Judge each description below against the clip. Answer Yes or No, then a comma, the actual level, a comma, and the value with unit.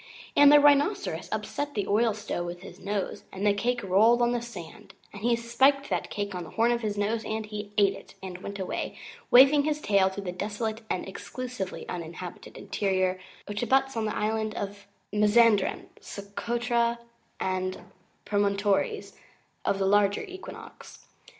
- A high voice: Yes, high, 210 Hz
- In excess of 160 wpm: Yes, average, 170 wpm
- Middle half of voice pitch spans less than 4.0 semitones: Yes, average, 3.3 semitones